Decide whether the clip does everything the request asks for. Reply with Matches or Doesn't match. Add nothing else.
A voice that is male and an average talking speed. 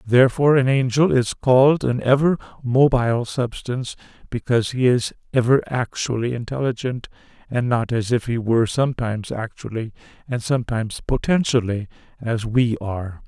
Doesn't match